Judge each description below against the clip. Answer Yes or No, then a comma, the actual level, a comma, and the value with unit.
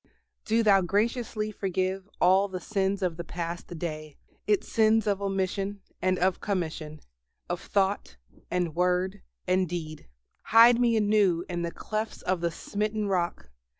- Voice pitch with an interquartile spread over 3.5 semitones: No, average, 3.0 semitones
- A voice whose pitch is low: No, high, 190 Hz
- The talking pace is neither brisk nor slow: Yes, average, 150 wpm